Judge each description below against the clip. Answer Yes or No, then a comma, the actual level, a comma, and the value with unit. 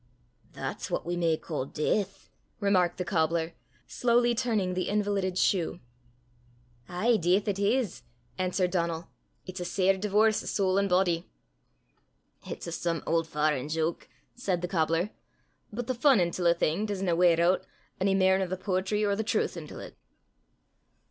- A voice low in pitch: No, medium, 185 Hz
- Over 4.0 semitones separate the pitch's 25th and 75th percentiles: No, average, 3.1 semitones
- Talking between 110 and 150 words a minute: No, average, 160 wpm